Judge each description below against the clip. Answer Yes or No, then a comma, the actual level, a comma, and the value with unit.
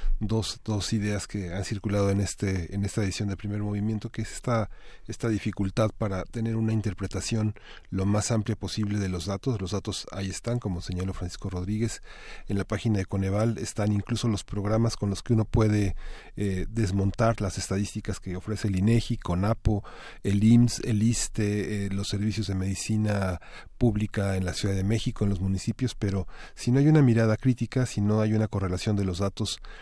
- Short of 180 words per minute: No, fast, 190 wpm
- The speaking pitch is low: Yes, low, 105 Hz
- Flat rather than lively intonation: Yes, narrow, 2.2 semitones